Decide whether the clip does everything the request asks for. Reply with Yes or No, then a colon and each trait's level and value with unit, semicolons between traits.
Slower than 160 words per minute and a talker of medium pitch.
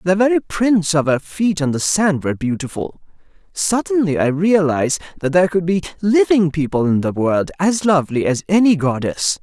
No: average, 180 wpm; medium, 170 Hz